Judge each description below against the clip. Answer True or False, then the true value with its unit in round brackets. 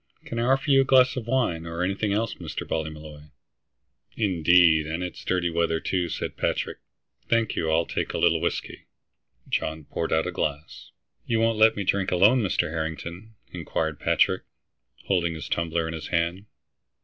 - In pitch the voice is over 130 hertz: False (85 Hz)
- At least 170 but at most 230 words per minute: True (175 wpm)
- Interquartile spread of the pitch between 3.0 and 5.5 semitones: True (5.2 semitones)